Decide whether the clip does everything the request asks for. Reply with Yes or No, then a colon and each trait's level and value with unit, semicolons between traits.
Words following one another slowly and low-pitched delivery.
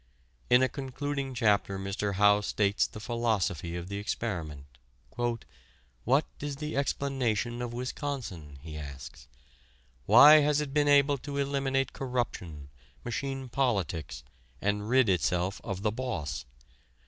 Yes: slow, 125 wpm; low, 115 Hz